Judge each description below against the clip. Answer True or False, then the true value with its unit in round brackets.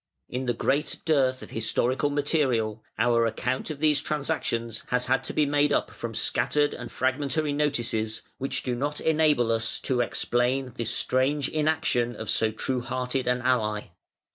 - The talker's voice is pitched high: False (130 Hz)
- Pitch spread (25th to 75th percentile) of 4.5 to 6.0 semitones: False (3.6 semitones)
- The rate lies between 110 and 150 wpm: False (160 wpm)